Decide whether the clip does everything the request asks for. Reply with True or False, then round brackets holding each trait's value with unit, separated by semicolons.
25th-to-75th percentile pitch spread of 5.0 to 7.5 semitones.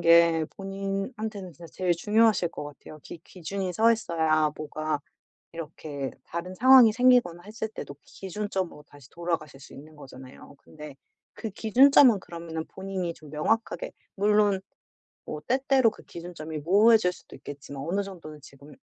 True (5.3 semitones)